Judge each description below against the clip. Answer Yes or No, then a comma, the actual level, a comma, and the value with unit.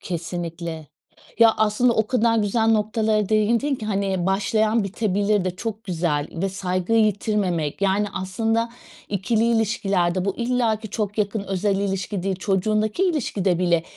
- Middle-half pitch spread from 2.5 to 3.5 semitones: Yes, average, 2.9 semitones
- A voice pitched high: Yes, high, 205 Hz